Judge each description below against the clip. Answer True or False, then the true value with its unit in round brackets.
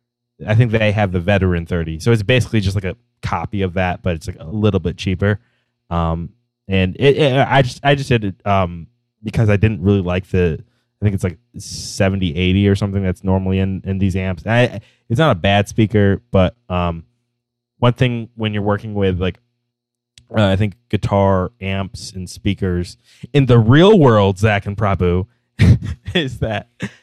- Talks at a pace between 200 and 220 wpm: False (185 wpm)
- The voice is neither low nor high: False (105 Hz)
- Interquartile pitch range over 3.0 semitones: True (4.1 semitones)